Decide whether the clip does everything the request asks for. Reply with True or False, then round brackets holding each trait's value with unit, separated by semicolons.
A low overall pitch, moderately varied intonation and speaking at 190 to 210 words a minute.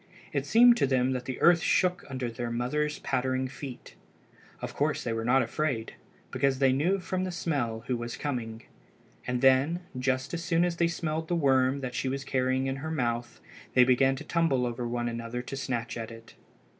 True (130 Hz; 4.0 semitones; 200 wpm)